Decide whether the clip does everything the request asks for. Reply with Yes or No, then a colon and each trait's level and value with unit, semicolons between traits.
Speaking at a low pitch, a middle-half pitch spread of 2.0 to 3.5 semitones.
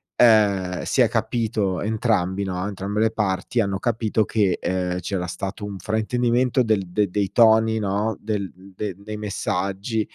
Yes: low, 105 Hz; narrow, 2.6 semitones